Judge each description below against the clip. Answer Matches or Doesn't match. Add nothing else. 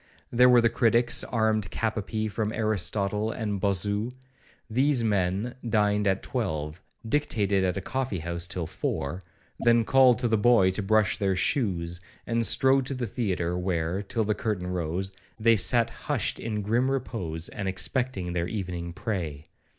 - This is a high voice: Doesn't match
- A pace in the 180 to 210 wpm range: Doesn't match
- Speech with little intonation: Doesn't match